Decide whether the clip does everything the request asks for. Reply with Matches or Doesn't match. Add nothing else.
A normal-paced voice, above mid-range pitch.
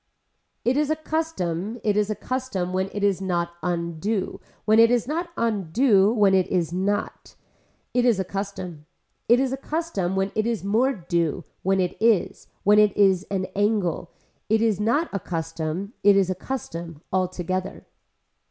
Matches